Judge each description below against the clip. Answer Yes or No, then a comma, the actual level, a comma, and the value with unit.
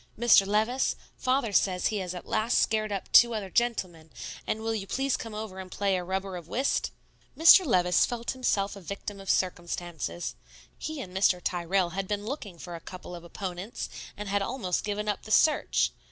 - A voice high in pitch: Yes, high, 200 Hz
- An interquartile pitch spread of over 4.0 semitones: No, average, 3.5 semitones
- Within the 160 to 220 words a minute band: Yes, average, 195 wpm